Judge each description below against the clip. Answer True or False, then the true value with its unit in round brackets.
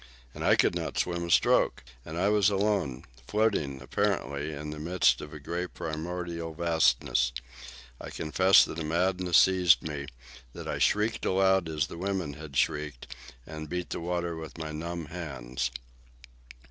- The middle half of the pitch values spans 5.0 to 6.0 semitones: False (3.1 semitones)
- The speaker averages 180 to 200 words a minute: False (160 wpm)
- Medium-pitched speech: False (85 Hz)